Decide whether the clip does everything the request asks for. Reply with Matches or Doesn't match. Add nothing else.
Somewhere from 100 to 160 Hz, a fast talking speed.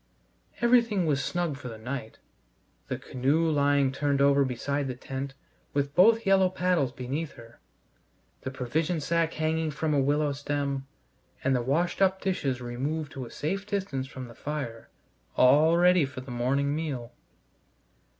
Doesn't match